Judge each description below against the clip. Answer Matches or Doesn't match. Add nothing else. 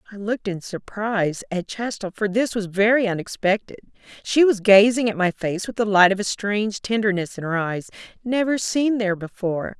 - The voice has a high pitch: Matches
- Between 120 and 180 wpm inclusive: Doesn't match